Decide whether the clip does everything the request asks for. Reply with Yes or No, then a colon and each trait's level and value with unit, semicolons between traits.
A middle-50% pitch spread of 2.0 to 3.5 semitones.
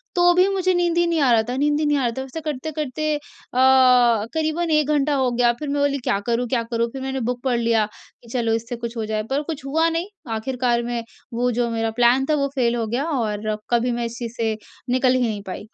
No: average, 4.0 semitones